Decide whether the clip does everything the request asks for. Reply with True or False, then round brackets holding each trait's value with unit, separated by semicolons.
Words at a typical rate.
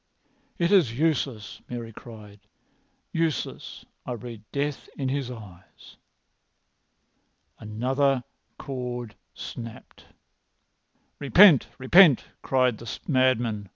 False (90 wpm)